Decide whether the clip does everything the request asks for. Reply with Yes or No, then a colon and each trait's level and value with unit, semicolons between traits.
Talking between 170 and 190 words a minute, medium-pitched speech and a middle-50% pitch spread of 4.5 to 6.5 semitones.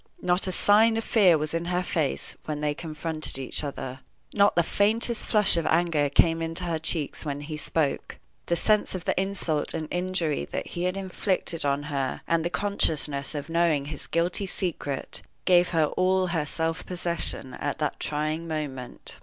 No: average, 180 wpm; medium, 165 Hz; average, 3.4 semitones